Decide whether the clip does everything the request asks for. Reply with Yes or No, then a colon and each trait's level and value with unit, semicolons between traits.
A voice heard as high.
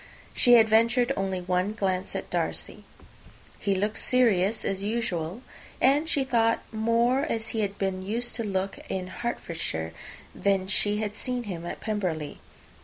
Yes: high, 210 Hz